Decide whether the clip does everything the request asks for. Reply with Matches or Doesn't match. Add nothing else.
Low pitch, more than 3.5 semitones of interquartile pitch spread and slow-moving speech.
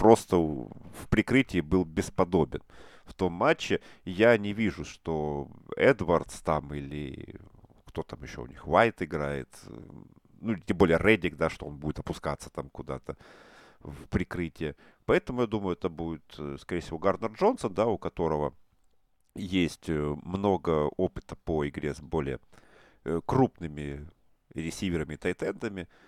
Doesn't match